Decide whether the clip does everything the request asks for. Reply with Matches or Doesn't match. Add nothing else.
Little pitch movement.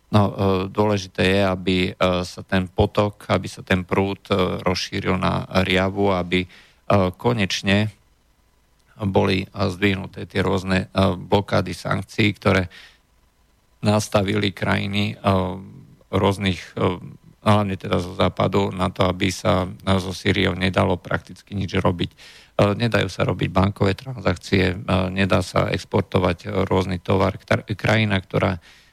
Matches